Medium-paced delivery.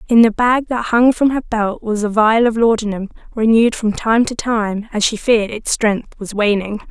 No: fast, 215 wpm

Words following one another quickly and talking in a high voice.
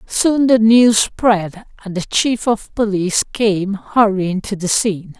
No: average, 160 wpm; high, 210 Hz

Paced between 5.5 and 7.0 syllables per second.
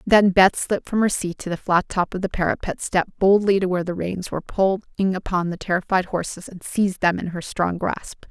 Yes: 5.6 syllables/s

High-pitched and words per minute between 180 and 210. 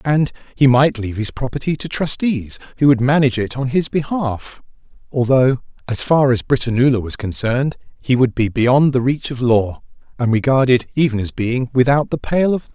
No: low, 130 Hz; average, 190 wpm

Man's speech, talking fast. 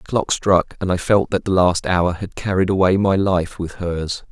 Yes: male; fast, 235 wpm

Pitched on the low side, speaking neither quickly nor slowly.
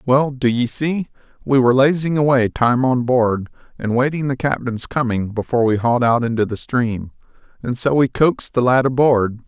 Yes: low, 125 Hz; average, 190 wpm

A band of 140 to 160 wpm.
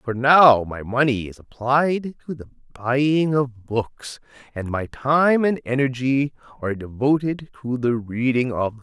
Yes: average, 155 wpm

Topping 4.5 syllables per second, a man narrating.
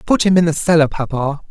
Yes: 6.1 syllables/s; male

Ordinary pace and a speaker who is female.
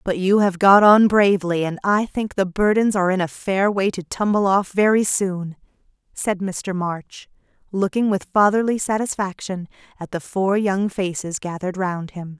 Yes: average, 175 wpm; female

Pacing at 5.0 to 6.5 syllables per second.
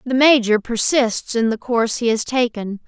No: 4.7 syllables/s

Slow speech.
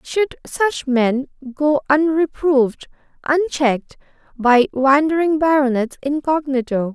Yes: slow, 85 wpm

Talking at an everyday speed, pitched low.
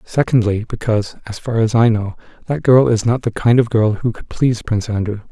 No: fast, 225 wpm; low, 115 Hz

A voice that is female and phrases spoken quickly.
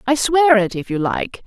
Yes: female; fast, 245 wpm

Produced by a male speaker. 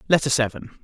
Yes: male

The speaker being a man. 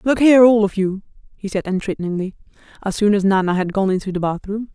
No: female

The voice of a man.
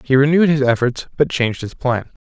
Yes: male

